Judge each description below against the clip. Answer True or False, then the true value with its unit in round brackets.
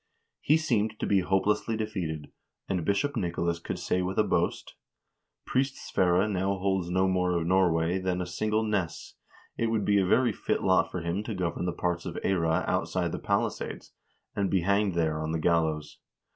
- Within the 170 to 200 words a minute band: True (185 wpm)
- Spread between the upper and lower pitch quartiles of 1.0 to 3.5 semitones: True (3.1 semitones)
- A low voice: True (95 Hz)